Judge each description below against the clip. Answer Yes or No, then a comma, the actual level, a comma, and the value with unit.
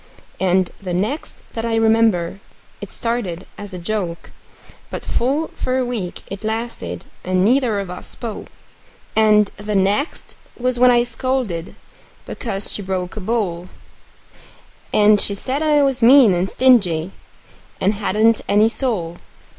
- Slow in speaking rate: No, average, 145 wpm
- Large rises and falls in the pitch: No, average, 4.4 semitones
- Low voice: No, high, 215 Hz